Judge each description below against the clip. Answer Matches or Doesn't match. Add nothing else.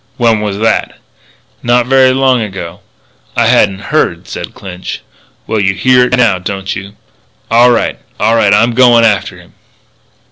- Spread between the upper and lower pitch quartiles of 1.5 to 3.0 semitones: Doesn't match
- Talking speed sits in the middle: Matches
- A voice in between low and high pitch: Doesn't match